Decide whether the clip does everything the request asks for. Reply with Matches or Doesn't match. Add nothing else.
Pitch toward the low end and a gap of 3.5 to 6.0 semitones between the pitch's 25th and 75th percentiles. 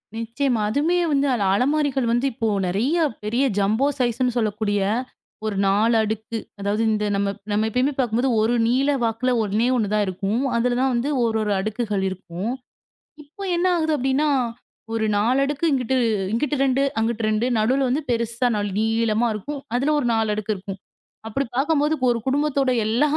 Doesn't match